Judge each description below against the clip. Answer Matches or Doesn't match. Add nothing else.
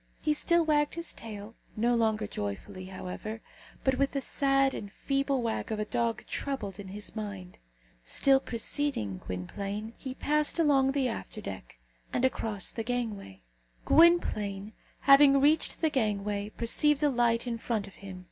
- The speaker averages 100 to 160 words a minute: Matches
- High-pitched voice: Matches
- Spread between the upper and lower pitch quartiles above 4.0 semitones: Matches